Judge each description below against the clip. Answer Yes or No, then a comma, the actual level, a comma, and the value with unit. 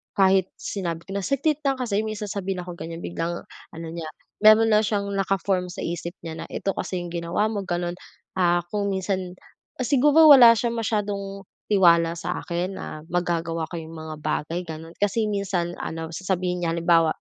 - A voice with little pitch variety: No, average, 3.3 semitones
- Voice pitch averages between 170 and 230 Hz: Yes, medium, 185 Hz